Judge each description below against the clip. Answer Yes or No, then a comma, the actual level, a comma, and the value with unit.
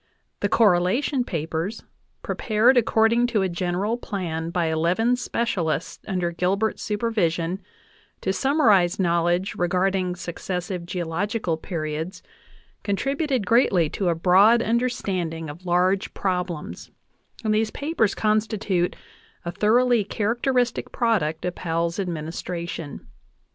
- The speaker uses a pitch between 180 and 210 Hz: Yes, high, 190 Hz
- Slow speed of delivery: Yes, slow, 115 wpm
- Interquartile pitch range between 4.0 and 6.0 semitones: Yes, average, 4.5 semitones